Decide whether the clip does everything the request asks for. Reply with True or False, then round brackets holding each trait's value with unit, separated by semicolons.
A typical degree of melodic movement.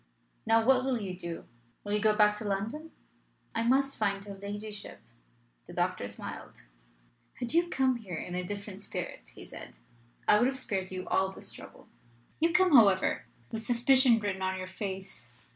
True (4.6 semitones)